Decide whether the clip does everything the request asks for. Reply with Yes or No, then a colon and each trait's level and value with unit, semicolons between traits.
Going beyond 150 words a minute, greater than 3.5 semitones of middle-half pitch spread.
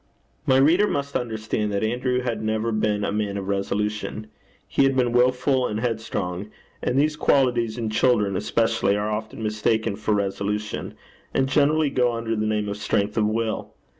No: average, 170 wpm; average, 3.0 semitones